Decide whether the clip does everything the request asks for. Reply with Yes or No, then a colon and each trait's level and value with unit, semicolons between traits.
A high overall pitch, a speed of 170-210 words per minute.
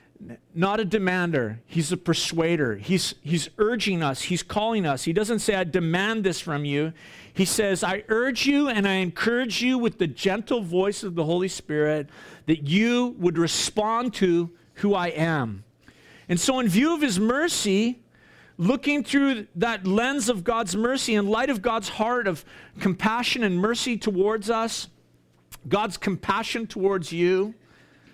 No: high, 195 Hz; average, 160 wpm